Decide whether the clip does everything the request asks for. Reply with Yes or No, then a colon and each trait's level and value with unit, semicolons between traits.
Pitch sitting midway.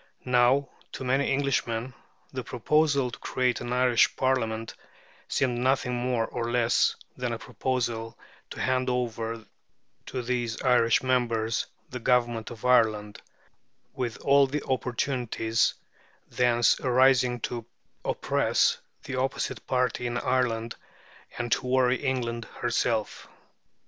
No: low, 125 Hz